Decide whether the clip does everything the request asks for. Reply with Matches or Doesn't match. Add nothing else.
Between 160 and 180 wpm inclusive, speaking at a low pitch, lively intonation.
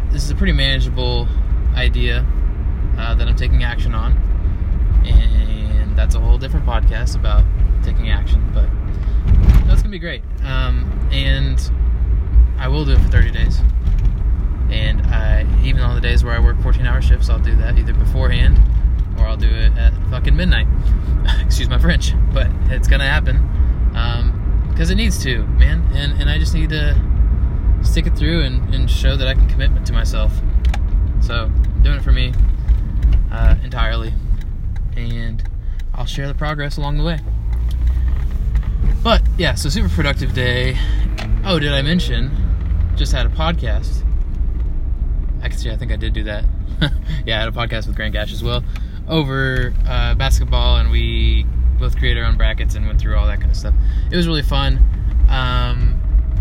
Matches